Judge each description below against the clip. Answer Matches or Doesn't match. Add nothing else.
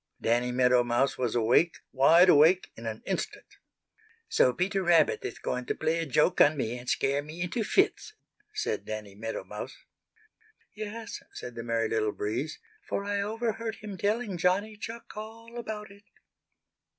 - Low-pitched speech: Doesn't match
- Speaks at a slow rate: Doesn't match